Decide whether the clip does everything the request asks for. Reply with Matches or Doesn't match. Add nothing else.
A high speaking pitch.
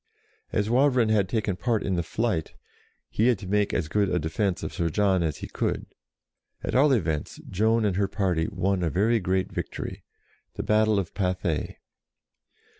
Doesn't match